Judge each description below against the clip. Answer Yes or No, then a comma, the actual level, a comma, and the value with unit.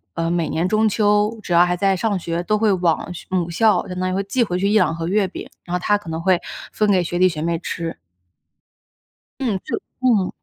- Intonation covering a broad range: No, average, 3.2 semitones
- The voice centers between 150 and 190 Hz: Yes, medium, 185 Hz